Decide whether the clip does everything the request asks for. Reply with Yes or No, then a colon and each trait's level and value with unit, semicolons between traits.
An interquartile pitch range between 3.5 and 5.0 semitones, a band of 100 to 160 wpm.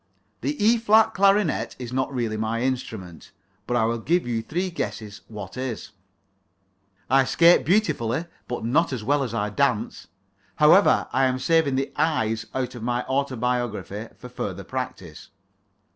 Yes: average, 4.0 semitones; average, 155 wpm